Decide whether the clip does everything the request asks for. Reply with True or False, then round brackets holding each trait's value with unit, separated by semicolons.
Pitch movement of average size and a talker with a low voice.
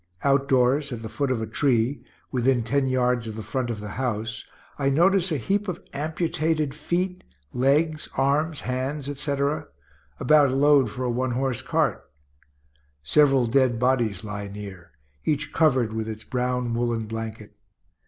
True (4.0 semitones; 130 Hz)